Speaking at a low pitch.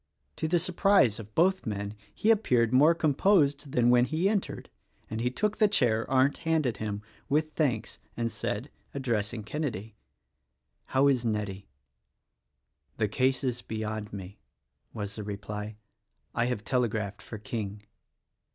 Yes: low, 120 Hz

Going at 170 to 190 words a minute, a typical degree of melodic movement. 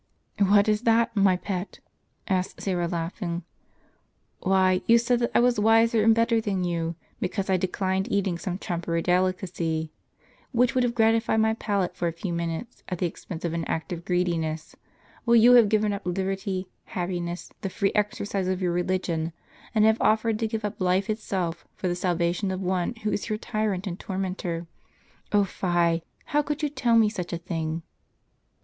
Yes: average, 185 wpm; average, 3.7 semitones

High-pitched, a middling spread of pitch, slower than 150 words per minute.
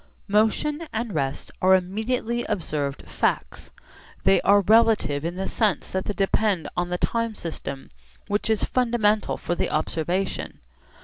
Yes: high, 200 Hz; average, 4.3 semitones; average, 140 wpm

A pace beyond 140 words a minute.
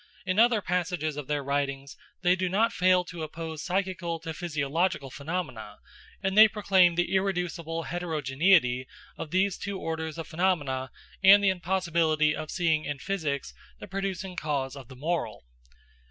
Yes: average, 155 wpm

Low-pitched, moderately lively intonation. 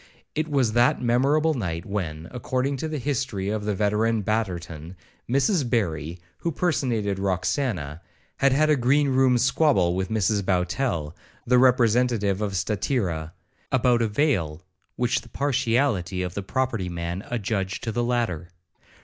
No: low, 110 Hz; wide, 5.8 semitones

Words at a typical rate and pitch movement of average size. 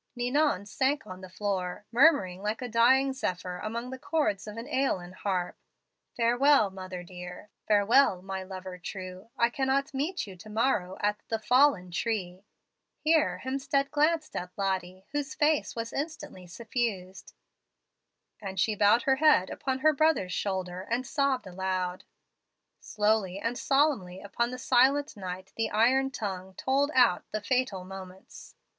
No: average, 150 wpm; wide, 6.1 semitones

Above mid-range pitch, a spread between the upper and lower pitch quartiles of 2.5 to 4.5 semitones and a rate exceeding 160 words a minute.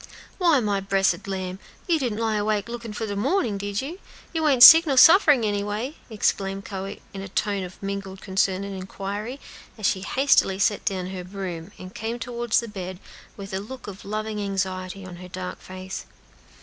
Yes: high, 200 Hz; average, 3.2 semitones; average, 190 wpm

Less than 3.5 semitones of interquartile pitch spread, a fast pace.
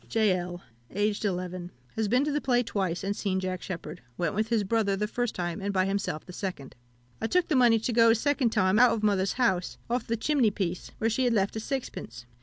No: average, 3.8 semitones; fast, 235 wpm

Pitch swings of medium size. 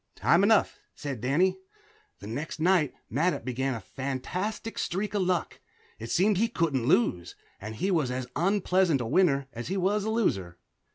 No: wide, 7.0 semitones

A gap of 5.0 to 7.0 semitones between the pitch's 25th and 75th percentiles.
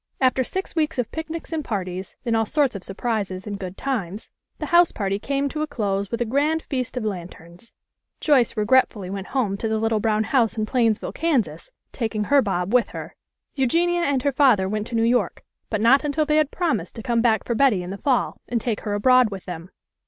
Yes: average, 5.3 semitones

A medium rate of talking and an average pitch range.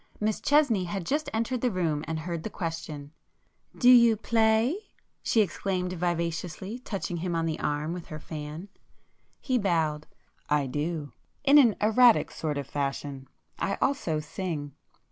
No: average, 150 wpm; wide, 6.2 semitones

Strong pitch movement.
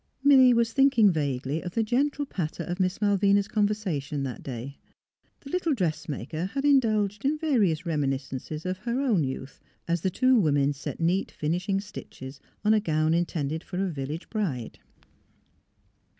Yes: wide, 6.5 semitones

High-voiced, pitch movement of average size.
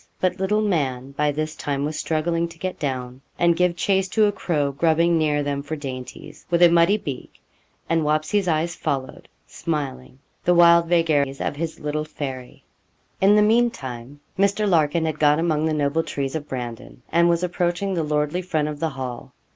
No: medium, 155 Hz; average, 3.4 semitones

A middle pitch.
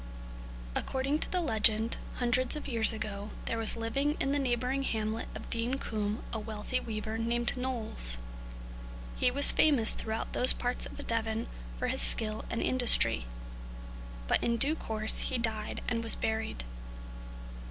No: high, 230 Hz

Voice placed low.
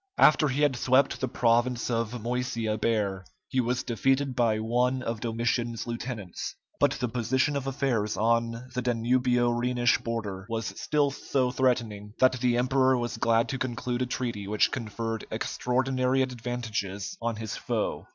Yes: low, 120 Hz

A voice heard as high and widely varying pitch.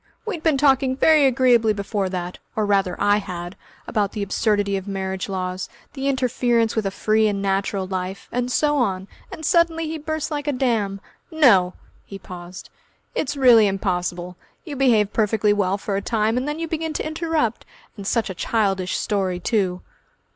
Yes: high, 210 Hz; wide, 5.7 semitones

